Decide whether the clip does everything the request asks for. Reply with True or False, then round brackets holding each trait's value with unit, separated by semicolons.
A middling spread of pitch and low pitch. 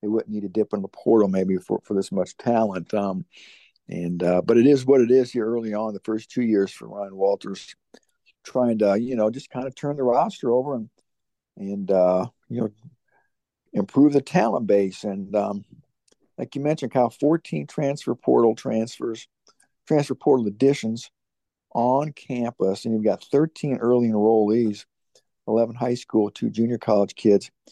True (3.8 semitones; 115 Hz)